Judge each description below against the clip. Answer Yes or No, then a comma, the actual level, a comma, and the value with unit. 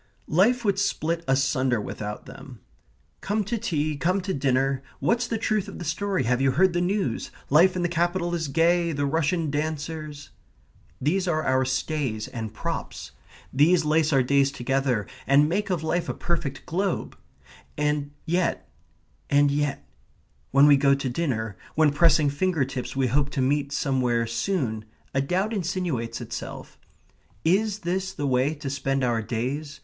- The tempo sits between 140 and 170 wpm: Yes, average, 165 wpm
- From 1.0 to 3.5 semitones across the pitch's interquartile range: No, average, 4.6 semitones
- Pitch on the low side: No, medium, 150 Hz